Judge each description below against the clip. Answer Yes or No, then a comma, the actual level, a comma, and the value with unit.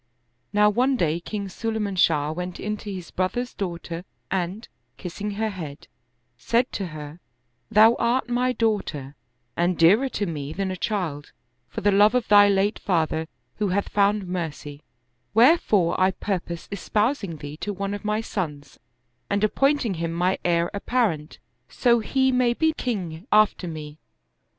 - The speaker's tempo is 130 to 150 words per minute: No, average, 160 wpm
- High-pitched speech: Yes, high, 195 Hz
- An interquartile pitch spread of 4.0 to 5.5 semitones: Yes, average, 4.5 semitones